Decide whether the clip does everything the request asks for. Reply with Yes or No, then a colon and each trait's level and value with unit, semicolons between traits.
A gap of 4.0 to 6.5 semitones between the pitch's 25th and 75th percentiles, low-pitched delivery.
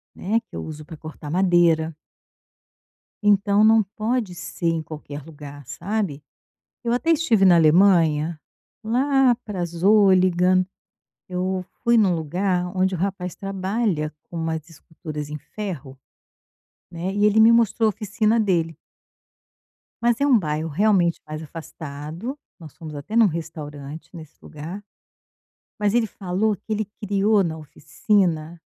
No: average, 4.9 semitones; medium, 180 Hz